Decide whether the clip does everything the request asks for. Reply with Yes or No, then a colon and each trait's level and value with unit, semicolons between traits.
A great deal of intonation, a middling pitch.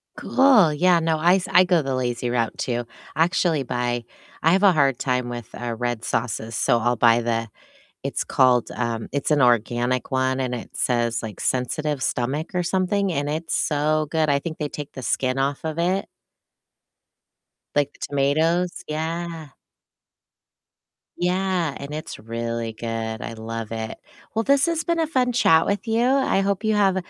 Yes: wide, 6.5 semitones; medium, 145 Hz